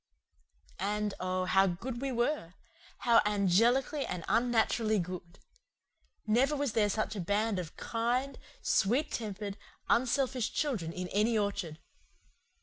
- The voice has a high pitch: Yes, high, 215 Hz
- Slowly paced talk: Yes, slow, 125 wpm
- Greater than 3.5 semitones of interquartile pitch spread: Yes, average, 4.2 semitones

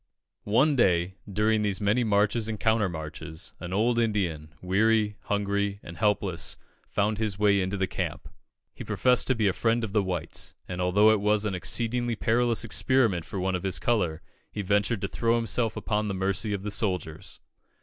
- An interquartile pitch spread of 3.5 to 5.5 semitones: No, average, 3.0 semitones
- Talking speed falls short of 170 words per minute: No, average, 180 wpm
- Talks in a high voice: No, low, 105 Hz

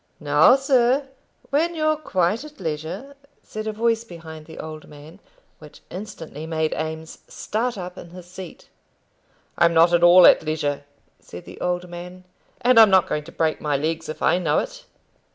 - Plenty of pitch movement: Yes, wide, 5.8 semitones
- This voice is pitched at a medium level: Yes, medium, 175 Hz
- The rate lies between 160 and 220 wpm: Yes, average, 175 wpm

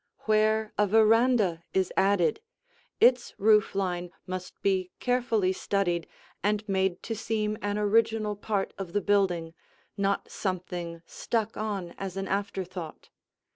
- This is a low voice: No, high, 200 Hz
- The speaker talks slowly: Yes, slow, 130 wpm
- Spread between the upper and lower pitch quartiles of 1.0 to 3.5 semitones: Yes, average, 2.7 semitones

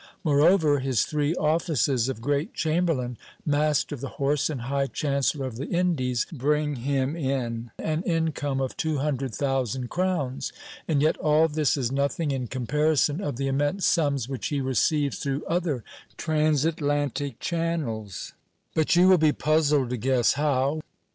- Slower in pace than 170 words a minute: Yes, average, 155 wpm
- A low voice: No, medium, 145 Hz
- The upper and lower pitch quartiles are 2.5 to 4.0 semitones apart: Yes, average, 2.8 semitones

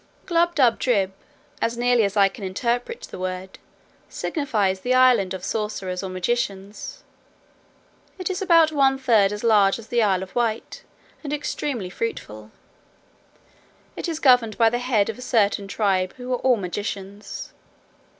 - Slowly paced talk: No, average, 150 wpm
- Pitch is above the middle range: Yes, high, 225 Hz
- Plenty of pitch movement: No, average, 4.6 semitones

